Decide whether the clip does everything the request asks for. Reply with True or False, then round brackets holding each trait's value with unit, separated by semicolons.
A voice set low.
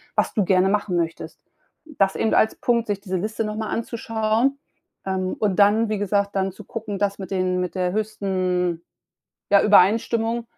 False (205 Hz)